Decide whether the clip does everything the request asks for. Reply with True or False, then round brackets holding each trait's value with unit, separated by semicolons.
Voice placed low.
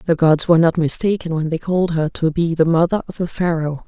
False (165 Hz)